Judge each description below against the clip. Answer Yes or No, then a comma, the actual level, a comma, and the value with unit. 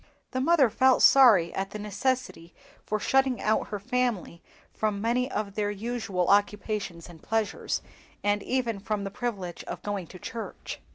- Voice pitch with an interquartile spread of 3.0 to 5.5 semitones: Yes, average, 3.7 semitones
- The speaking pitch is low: No, high, 210 Hz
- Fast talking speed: No, average, 160 wpm